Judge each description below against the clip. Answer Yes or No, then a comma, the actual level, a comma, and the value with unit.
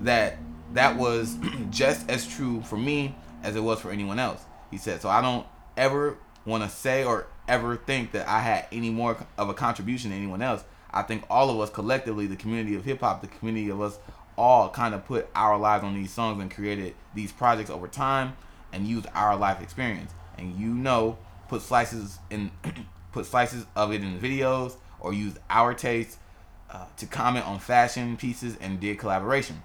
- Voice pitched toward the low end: Yes, low, 110 Hz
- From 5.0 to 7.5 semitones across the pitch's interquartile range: No, average, 3.6 semitones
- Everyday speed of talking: Yes, average, 195 wpm